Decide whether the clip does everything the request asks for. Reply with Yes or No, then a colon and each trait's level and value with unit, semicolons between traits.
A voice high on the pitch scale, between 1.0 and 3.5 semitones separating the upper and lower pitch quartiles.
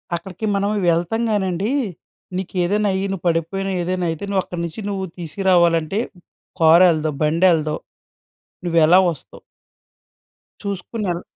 No: medium, 180 Hz; average, 2.8 semitones